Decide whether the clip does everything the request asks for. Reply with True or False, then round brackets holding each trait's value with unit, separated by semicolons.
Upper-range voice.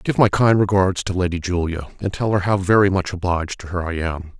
False (90 Hz)